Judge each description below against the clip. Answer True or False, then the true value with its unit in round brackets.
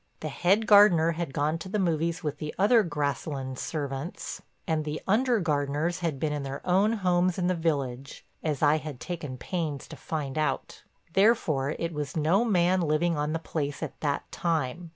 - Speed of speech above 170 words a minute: True (185 wpm)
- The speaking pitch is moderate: True (160 Hz)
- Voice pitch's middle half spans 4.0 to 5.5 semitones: False (3.4 semitones)